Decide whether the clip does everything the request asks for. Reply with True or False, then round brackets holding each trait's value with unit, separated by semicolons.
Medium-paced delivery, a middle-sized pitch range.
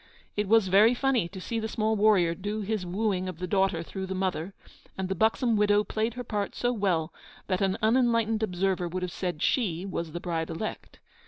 False (210 wpm; 3.2 semitones)